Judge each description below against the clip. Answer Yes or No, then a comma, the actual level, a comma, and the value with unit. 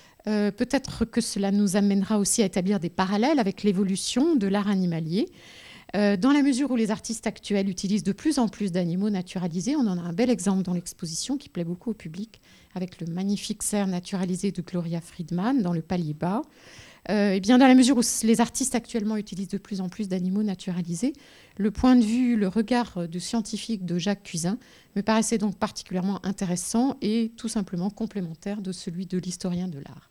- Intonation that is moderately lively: Yes, average, 3.6 semitones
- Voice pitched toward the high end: Yes, high, 205 Hz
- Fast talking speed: No, average, 195 wpm